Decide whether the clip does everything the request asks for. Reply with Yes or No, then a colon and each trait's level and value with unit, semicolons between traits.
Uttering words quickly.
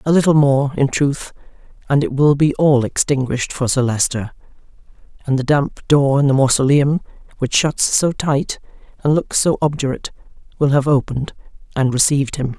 No: average, 165 wpm